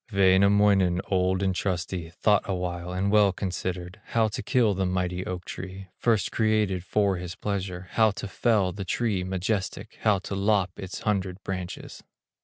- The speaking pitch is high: No, very low, 95 Hz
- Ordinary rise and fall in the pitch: No, narrow, 2.0 semitones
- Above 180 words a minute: No, average, 160 wpm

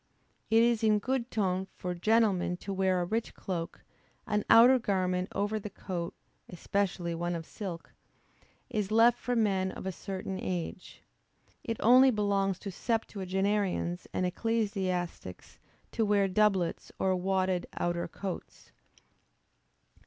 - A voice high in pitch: Yes, high, 195 Hz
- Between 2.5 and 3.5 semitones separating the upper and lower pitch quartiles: Yes, average, 3.0 semitones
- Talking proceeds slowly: Yes, slow, 130 wpm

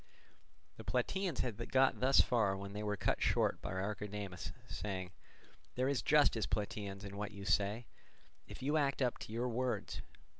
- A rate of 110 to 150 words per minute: No, average, 165 wpm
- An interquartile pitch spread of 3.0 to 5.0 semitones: Yes, average, 4.3 semitones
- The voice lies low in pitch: Yes, low, 105 Hz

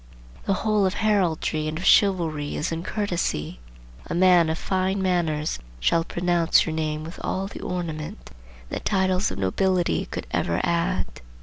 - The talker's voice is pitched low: No, medium, 175 Hz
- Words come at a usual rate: Yes, average, 160 wpm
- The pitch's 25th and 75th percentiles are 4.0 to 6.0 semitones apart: No, average, 3.1 semitones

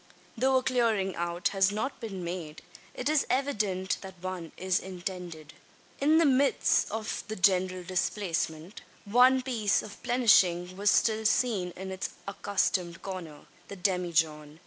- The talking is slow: No, average, 145 wpm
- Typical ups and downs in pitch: Yes, average, 3.8 semitones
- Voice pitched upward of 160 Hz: Yes, high, 190 Hz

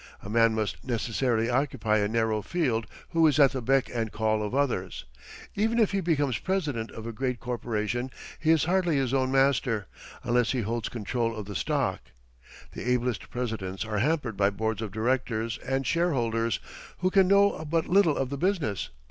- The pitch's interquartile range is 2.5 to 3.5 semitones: No, average, 4.5 semitones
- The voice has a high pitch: No, low, 125 Hz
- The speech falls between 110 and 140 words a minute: No, average, 180 wpm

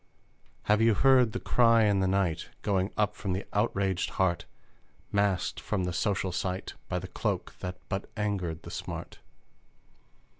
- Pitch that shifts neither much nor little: No, narrow, 2.3 semitones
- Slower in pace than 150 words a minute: No, average, 155 wpm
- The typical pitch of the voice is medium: No, very low, 95 Hz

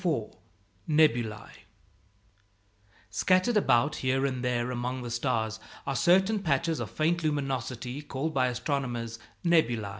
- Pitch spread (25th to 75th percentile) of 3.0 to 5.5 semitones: Yes, average, 4.5 semitones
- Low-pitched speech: Yes, low, 130 Hz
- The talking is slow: Yes, slow, 120 wpm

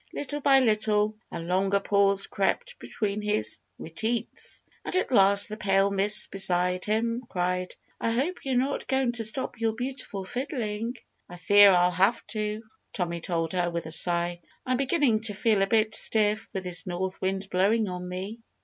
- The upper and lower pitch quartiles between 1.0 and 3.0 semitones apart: No, average, 3.9 semitones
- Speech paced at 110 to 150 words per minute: No, average, 175 wpm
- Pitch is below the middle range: No, high, 205 Hz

